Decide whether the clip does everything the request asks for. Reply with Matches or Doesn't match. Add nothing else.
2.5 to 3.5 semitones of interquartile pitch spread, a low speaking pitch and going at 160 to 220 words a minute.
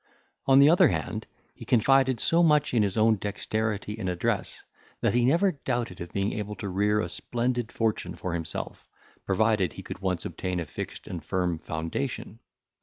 Doesn't match